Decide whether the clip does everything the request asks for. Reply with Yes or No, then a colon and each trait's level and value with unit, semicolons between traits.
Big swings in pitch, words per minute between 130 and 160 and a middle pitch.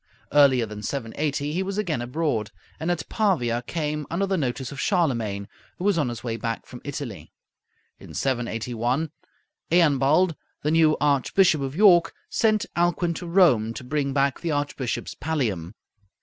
Yes: wide, 5.7 semitones; average, 155 wpm; medium, 145 Hz